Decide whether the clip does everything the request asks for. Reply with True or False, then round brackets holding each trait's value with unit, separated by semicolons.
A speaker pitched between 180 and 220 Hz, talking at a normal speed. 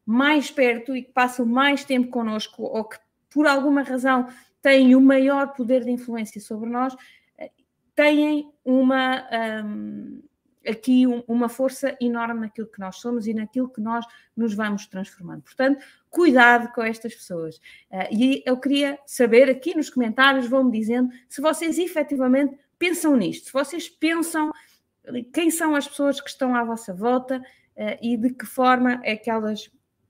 False (255 Hz; 155 wpm)